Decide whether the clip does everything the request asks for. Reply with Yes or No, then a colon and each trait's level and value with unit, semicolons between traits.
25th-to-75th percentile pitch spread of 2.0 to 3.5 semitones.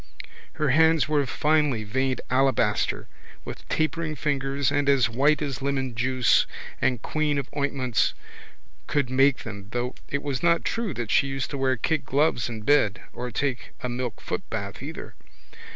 Yes: average, 2.8 semitones